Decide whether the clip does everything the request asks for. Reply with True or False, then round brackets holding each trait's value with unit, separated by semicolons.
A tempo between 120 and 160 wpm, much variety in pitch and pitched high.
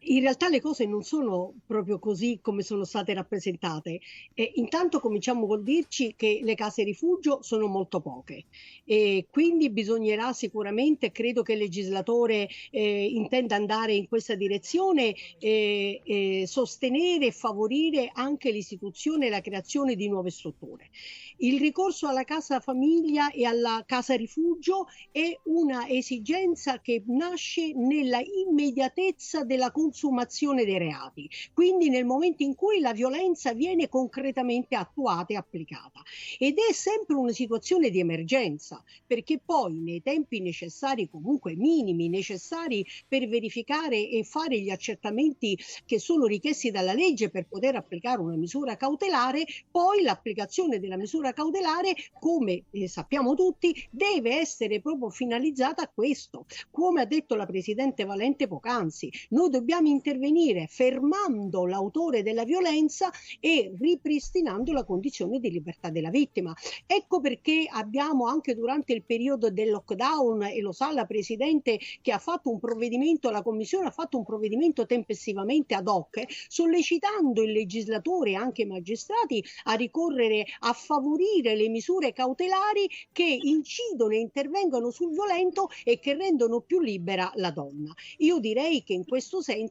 True (145 wpm; 6.3 semitones; 250 Hz)